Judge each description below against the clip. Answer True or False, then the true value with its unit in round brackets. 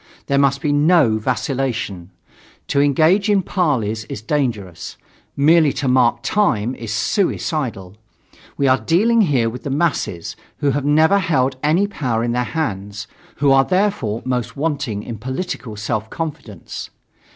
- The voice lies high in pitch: False (135 Hz)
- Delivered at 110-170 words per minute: True (145 wpm)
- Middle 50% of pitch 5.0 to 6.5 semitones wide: True (5.6 semitones)